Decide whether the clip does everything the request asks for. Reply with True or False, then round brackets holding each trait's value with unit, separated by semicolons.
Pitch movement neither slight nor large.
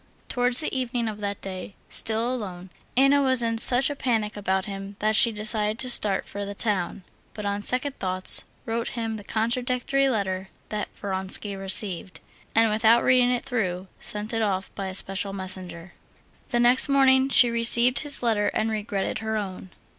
True (3.8 semitones)